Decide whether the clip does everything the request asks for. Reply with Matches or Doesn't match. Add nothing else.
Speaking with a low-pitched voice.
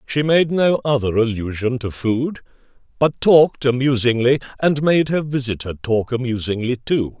Matches